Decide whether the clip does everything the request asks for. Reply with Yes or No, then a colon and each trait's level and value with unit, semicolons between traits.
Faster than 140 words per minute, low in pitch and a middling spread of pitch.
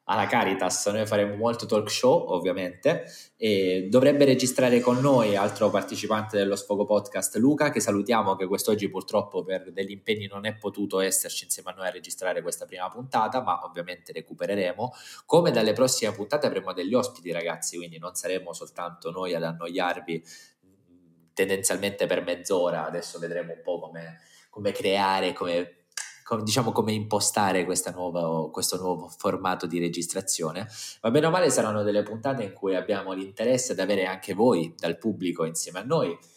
Yes: average, 160 wpm; very low, 95 Hz; average, 3.5 semitones